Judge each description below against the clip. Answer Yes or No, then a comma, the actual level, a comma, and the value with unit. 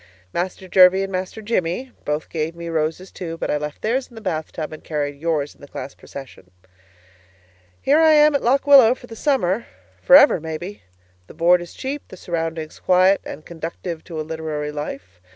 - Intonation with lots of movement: Yes, wide, 6.0 semitones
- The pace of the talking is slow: No, average, 195 wpm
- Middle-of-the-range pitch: Yes, medium, 170 Hz